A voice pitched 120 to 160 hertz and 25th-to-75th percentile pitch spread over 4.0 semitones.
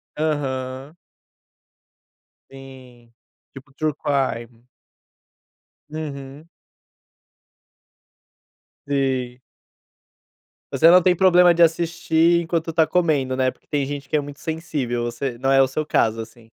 No: medium, 140 Hz; average, 3.7 semitones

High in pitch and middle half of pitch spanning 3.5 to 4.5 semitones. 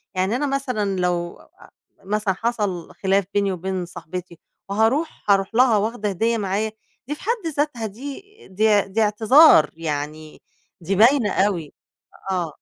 Yes: high, 205 Hz; average, 4.0 semitones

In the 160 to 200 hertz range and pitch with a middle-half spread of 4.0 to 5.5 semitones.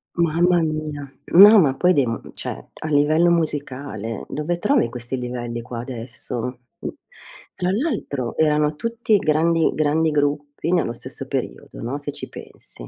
No: medium, 150 Hz; average, 4.7 semitones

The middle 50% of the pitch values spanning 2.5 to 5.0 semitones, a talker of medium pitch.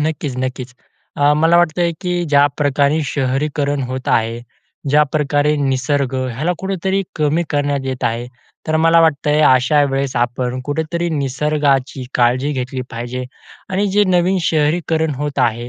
Yes: average, 3.4 semitones; medium, 145 Hz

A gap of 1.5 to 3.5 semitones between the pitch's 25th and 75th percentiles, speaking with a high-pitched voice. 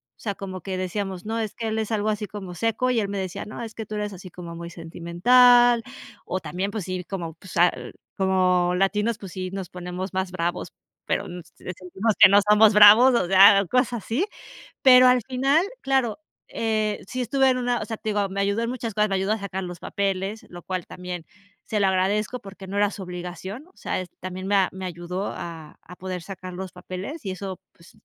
Yes: average, 3.2 semitones; high, 195 Hz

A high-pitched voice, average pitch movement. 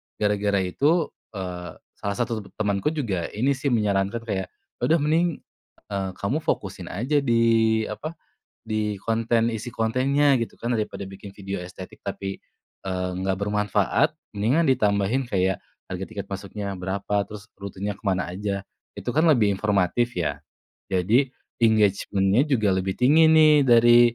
No: low, 105 Hz; average, 3.7 semitones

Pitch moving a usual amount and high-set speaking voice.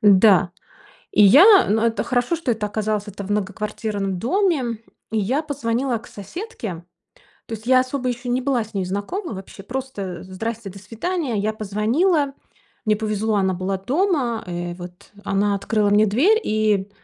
Yes: average, 4.3 semitones; high, 215 Hz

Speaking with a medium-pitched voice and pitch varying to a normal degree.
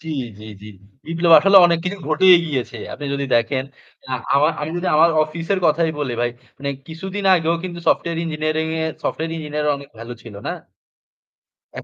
Yes: medium, 160 Hz; average, 3.1 semitones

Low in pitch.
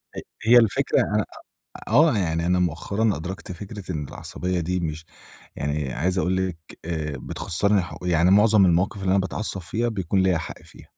Yes: very low, 90 Hz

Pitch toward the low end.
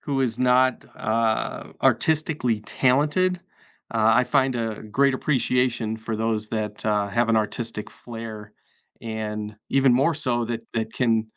Yes: low, 115 Hz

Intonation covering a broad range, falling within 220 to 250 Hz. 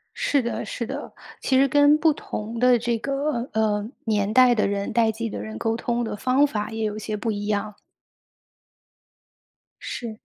No: average, 3.2 semitones; high, 230 Hz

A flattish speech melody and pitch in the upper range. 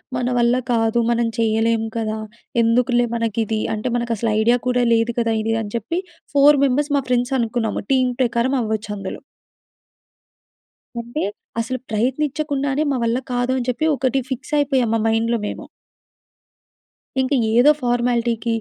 Yes: narrow, 2.1 semitones; high, 235 Hz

